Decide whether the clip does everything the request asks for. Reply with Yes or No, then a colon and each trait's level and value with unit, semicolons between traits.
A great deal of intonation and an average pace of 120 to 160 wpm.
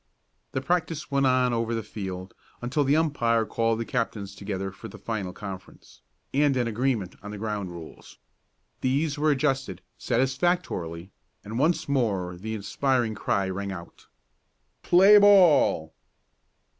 Yes: wide, 5.9 semitones; average, 140 wpm